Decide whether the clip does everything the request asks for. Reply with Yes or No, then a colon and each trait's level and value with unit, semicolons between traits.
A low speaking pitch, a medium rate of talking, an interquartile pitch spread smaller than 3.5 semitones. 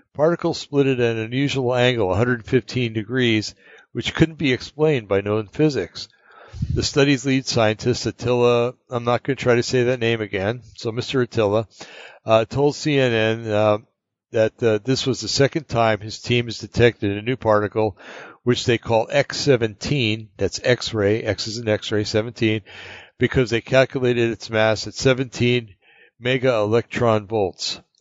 Yes: low, 120 Hz; average, 155 wpm; average, 3.0 semitones